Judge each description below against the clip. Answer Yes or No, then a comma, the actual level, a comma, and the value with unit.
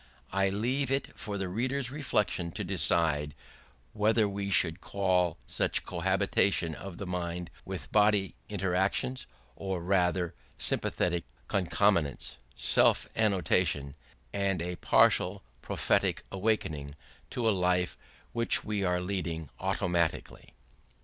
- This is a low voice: Yes, very low, 95 Hz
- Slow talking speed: Yes, slow, 115 wpm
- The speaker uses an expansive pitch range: No, average, 2.9 semitones